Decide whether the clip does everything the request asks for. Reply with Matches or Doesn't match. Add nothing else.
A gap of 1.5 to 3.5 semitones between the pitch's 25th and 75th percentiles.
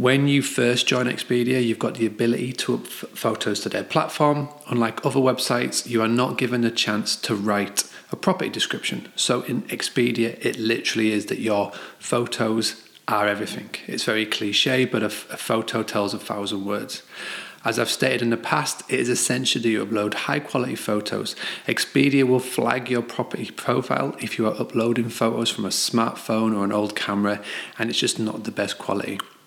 Matches